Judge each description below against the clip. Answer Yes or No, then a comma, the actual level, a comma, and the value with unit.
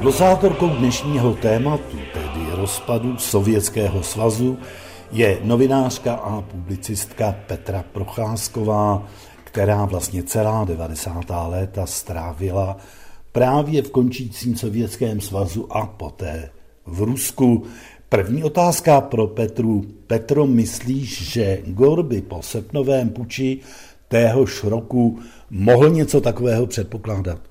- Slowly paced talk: Yes, slow, 100 wpm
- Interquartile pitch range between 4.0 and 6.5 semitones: Yes, average, 4.4 semitones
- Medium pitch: No, low, 110 Hz